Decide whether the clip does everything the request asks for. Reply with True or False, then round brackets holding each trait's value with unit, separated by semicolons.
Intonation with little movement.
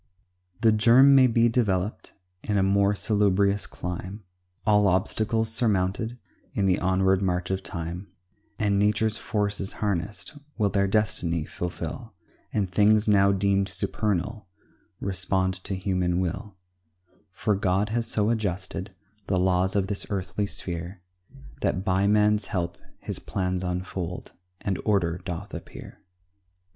True (2.2 semitones)